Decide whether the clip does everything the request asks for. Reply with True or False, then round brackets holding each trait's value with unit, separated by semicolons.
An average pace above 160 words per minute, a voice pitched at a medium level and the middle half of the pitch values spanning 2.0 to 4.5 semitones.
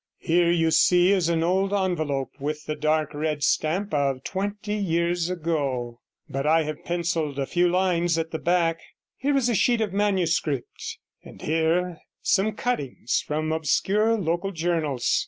False (155 wpm; 170 Hz; 3.5 semitones)